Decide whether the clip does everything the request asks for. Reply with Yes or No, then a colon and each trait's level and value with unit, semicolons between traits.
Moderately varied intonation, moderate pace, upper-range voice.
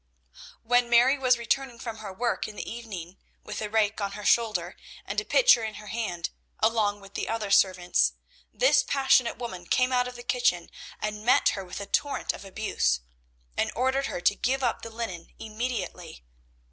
Yes: average, 3.6 semitones; average, 185 wpm; high, 220 Hz